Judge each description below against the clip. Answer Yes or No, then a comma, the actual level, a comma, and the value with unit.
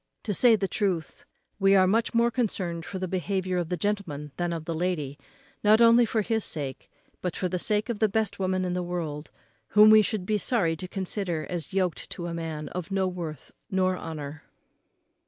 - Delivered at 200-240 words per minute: Yes, fast, 205 wpm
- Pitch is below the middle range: No, medium, 185 Hz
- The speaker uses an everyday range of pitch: Yes, average, 3.7 semitones